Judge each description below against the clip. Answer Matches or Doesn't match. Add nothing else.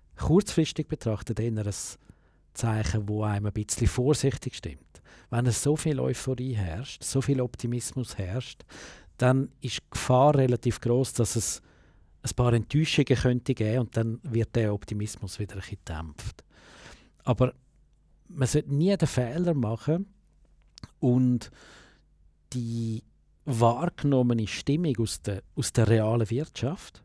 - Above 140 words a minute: Doesn't match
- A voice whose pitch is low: Matches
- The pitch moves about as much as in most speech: Matches